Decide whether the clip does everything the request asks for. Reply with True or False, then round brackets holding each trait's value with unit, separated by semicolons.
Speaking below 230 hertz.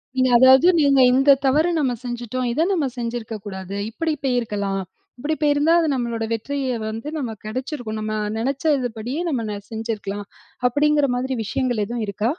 False (245 Hz)